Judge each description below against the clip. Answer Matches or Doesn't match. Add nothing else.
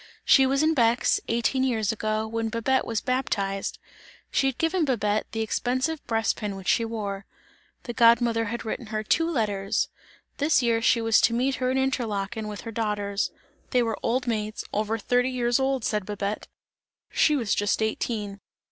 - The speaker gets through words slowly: Doesn't match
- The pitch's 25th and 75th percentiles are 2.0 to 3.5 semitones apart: Matches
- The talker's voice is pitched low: Doesn't match